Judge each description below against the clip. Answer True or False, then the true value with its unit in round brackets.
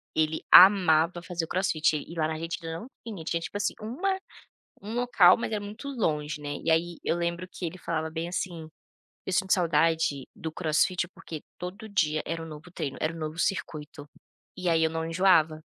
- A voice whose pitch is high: False (165 Hz)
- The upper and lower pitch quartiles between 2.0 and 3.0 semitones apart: True (2.7 semitones)